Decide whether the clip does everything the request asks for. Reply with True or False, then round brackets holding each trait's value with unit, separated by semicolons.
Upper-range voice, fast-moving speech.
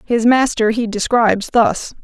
False (230 Hz; 150 wpm)